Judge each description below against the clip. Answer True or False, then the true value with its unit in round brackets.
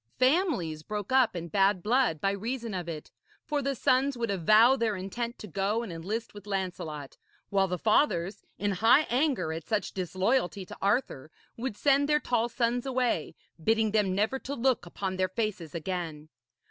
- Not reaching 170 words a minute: False (175 wpm)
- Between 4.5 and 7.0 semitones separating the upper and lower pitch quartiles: True (5.0 semitones)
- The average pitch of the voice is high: True (210 Hz)